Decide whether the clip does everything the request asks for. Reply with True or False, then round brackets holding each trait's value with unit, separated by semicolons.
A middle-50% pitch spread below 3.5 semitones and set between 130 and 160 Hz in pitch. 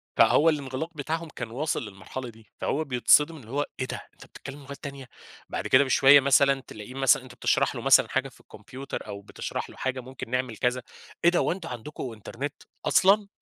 True (2.9 semitones; 135 Hz)